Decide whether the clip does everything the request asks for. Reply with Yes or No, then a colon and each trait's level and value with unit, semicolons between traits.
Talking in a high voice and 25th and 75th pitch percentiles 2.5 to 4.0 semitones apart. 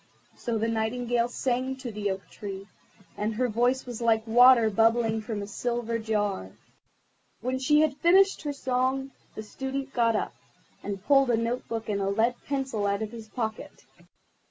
Yes: high, 230 Hz; average, 3.0 semitones